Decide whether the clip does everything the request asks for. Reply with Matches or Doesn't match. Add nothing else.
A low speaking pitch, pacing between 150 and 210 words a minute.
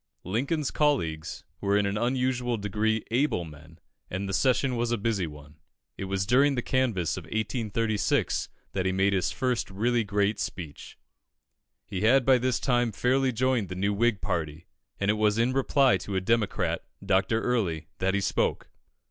Matches